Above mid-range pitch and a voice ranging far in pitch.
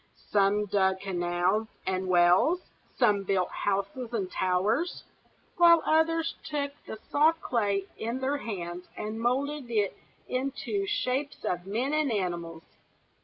Yes: high, 215 Hz; wide, 6.9 semitones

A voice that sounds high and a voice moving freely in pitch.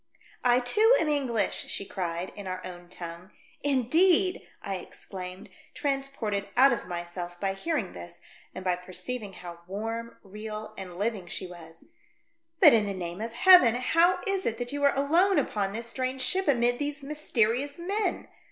Yes: high, 230 Hz; wide, 7.3 semitones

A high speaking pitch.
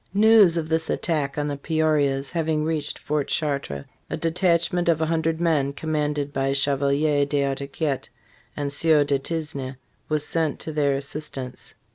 No: medium, 150 Hz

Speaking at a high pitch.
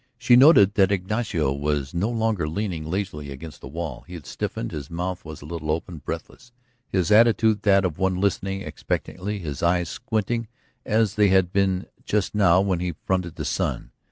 No: very low, 95 Hz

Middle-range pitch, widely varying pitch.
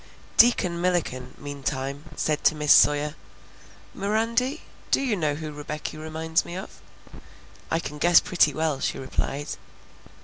No: medium, 155 Hz; average, 3.5 semitones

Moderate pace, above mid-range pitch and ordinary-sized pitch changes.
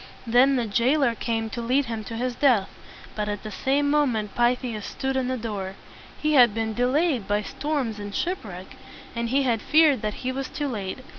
No: fast, 210 wpm; high, 240 Hz; average, 3.8 semitones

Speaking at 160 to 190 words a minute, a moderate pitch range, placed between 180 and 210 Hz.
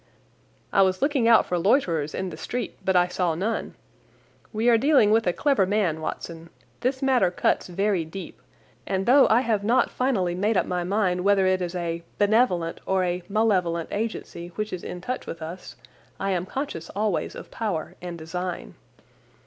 Yes: average, 180 wpm; average, 4.1 semitones; high, 190 Hz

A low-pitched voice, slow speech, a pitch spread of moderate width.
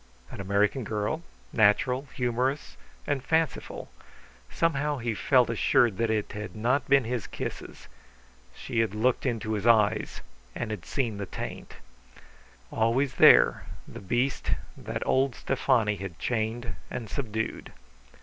Yes: low, 115 Hz; slow, 130 wpm; average, 3.5 semitones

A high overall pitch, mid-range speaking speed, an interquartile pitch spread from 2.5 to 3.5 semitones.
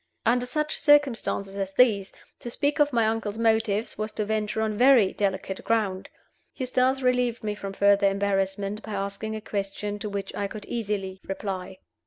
Yes: high, 210 Hz; average, 170 wpm; average, 2.8 semitones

